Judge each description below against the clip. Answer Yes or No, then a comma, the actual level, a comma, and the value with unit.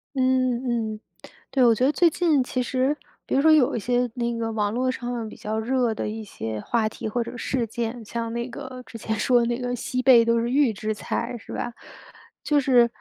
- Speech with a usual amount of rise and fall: No, narrow, 2.1 semitones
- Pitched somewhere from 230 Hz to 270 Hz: Yes, high, 240 Hz